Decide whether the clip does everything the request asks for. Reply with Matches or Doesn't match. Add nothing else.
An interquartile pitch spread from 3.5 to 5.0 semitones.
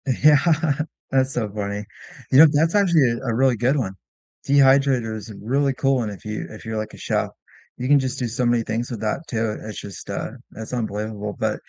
Matches